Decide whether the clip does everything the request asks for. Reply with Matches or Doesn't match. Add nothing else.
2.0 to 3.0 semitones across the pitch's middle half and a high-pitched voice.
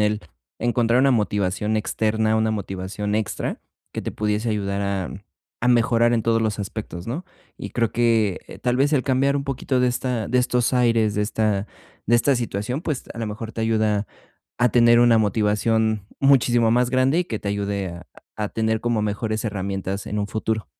Doesn't match